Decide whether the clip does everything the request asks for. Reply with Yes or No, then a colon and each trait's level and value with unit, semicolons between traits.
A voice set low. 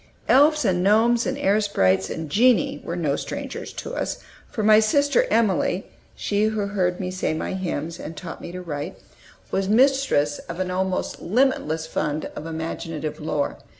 No: medium, 185 Hz